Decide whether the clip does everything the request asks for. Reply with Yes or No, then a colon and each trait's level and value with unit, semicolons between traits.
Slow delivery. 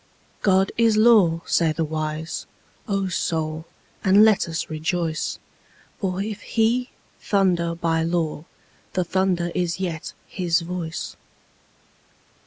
Yes: slow, 110 wpm